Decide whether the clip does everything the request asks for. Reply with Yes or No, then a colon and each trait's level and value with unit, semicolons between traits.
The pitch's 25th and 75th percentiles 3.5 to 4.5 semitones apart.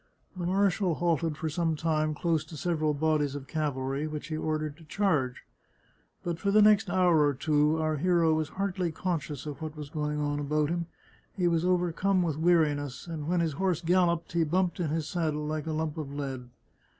No: narrow, 2.6 semitones